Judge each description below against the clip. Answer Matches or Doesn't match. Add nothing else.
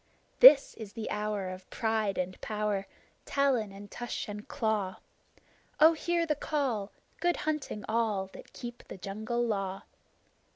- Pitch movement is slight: Doesn't match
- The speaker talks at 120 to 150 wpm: Matches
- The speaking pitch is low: Doesn't match